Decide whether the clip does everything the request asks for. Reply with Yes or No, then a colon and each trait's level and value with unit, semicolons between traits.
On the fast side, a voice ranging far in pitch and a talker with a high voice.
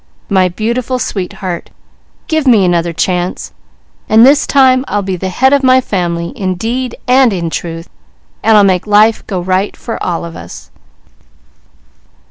No: average, 155 wpm; wide, 5.7 semitones; high, 200 Hz